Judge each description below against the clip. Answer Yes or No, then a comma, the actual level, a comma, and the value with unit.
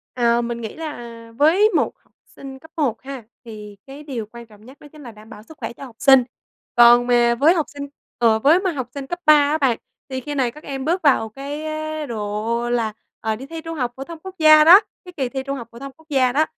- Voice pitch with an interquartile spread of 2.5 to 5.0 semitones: Yes, average, 4.5 semitones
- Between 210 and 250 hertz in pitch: No, very high, 270 Hz